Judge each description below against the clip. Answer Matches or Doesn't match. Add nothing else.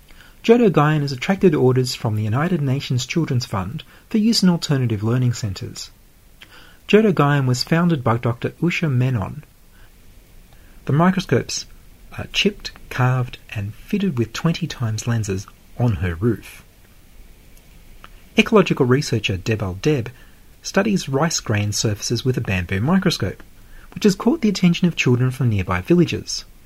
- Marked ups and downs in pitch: Matches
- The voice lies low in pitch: Matches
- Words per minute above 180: Doesn't match